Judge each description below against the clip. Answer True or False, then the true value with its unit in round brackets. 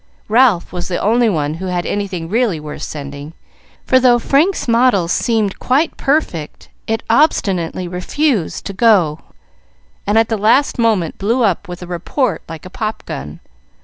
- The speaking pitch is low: False (200 Hz)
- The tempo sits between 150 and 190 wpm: True (160 wpm)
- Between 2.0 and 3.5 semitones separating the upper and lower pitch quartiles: False (5.5 semitones)